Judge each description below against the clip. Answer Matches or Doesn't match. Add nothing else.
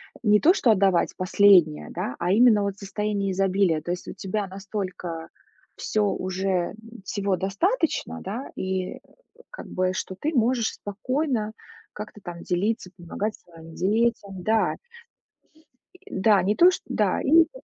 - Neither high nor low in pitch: Doesn't match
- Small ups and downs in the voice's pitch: Doesn't match